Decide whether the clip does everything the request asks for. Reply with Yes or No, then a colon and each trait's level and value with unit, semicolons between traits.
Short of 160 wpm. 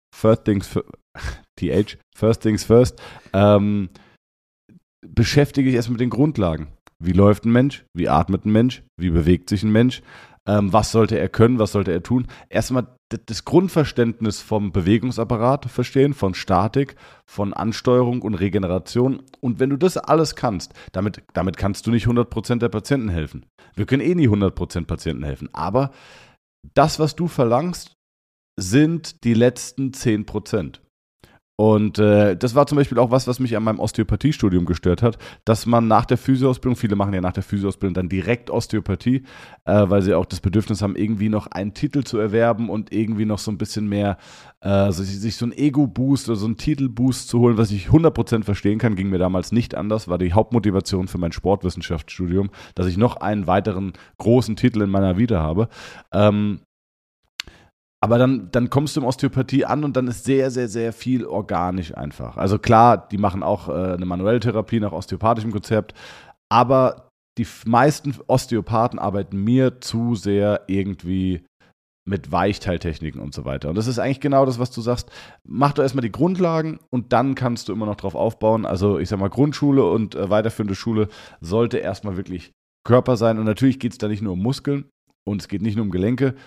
No: average, 185 wpm